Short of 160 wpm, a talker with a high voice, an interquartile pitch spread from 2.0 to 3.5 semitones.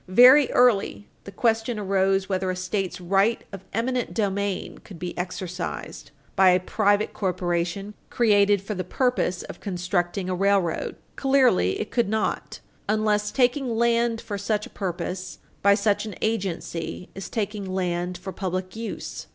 Yes: average, 150 wpm; high, 200 Hz; average, 3.0 semitones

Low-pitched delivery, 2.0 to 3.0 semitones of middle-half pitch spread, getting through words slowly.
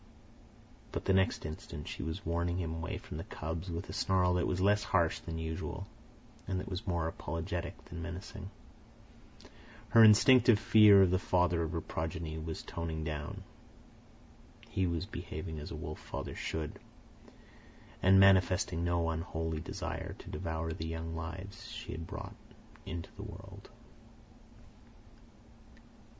No: very low, 85 Hz; narrow, 2.4 semitones; average, 145 wpm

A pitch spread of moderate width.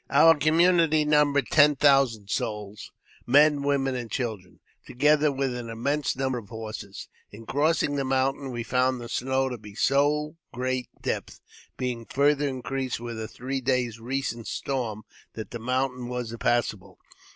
Yes: average, 3.4 semitones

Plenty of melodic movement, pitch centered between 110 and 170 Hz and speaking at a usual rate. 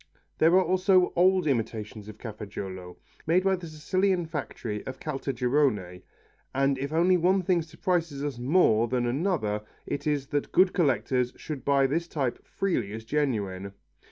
Yes: wide, 6.9 semitones; medium, 140 Hz; average, 150 wpm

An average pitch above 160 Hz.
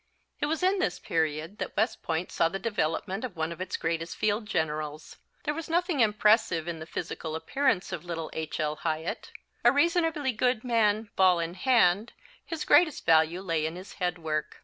Yes: medium, 185 Hz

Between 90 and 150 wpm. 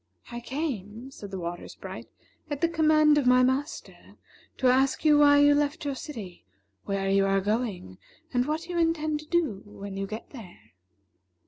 No: average, 180 wpm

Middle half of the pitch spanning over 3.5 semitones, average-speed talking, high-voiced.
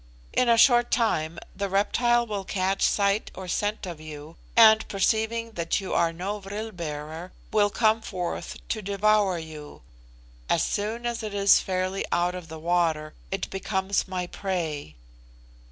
Yes: average, 4.0 semitones; average, 155 wpm; high, 195 Hz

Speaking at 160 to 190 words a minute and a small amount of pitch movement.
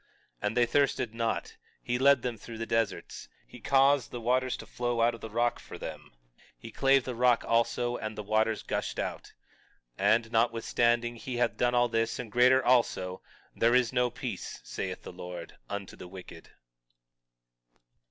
Yes: average, 180 wpm; narrow, 1.6 semitones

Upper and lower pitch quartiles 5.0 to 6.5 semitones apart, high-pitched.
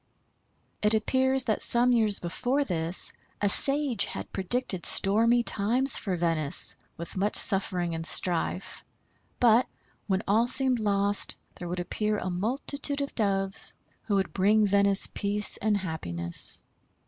No: average, 4.3 semitones; high, 205 Hz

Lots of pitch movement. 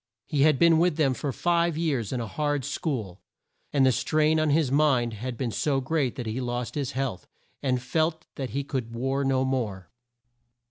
No: average, 3.8 semitones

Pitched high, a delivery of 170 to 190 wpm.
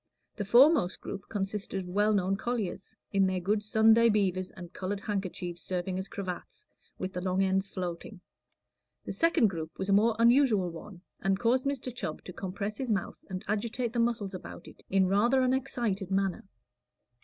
Yes: high, 200 Hz; average, 180 wpm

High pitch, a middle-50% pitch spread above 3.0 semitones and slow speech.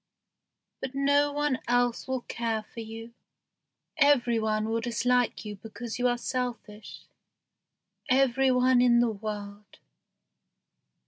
No: high, 240 Hz; narrow, 2.4 semitones; slow, 120 wpm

